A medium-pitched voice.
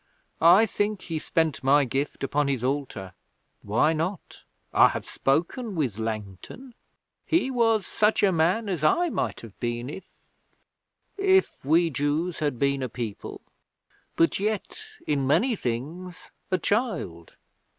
Yes: medium, 155 Hz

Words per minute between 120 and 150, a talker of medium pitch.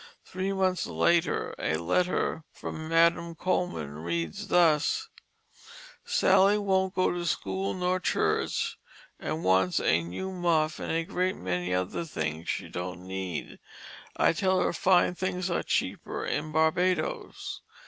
Yes: average, 140 wpm; medium, 165 Hz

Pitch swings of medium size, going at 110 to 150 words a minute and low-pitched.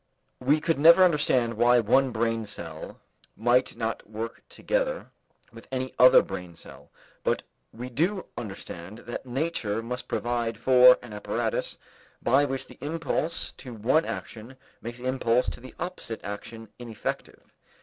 Yes: average, 3.1 semitones; average, 145 wpm; low, 120 Hz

